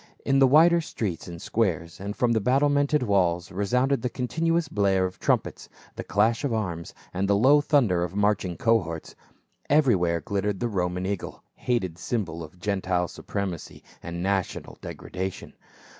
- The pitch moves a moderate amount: No, wide, 5.8 semitones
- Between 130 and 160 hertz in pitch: No, low, 100 Hz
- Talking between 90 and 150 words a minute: No, average, 160 wpm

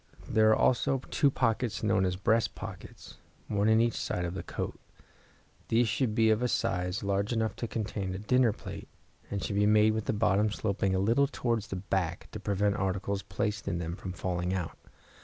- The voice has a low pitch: Yes, low, 105 Hz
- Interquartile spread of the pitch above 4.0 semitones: No, average, 2.8 semitones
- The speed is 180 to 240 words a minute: Yes, average, 200 wpm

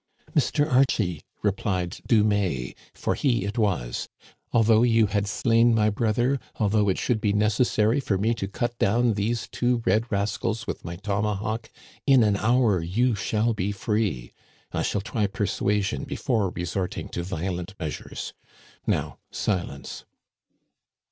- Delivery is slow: No, average, 150 wpm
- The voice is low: Yes, low, 105 Hz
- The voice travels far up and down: No, average, 3.0 semitones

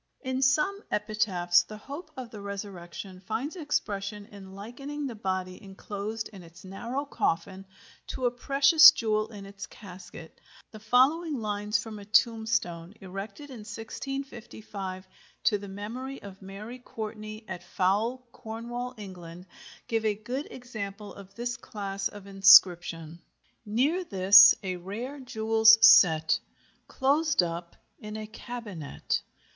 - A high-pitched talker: Yes, high, 210 Hz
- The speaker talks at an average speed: No, slow, 130 wpm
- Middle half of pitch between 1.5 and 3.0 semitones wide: No, average, 3.9 semitones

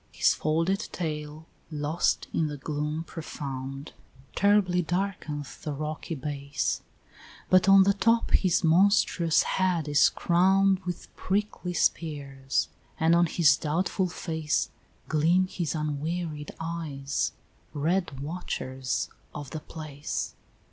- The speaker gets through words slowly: Yes, slow, 115 wpm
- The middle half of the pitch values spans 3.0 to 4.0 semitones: Yes, average, 3.4 semitones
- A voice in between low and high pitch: Yes, medium, 160 Hz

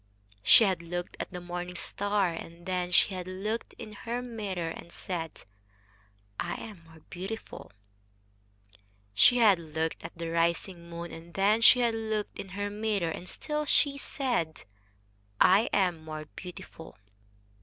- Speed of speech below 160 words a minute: Yes, average, 150 wpm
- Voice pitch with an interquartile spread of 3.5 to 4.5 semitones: Yes, average, 4.1 semitones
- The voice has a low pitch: No, medium, 185 Hz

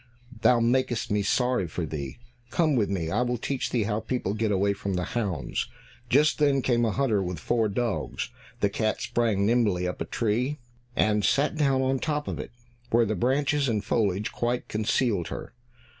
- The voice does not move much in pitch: No, average, 4.0 semitones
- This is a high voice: No, low, 115 Hz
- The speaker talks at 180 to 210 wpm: Yes, average, 190 wpm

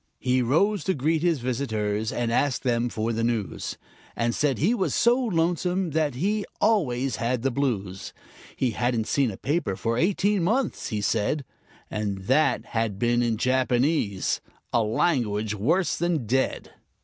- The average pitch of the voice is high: No, low, 125 Hz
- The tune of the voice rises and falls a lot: Yes, wide, 6.4 semitones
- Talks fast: No, average, 160 wpm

